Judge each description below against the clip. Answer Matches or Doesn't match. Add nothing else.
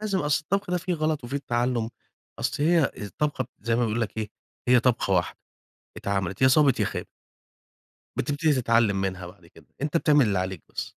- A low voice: Matches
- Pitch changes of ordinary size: Doesn't match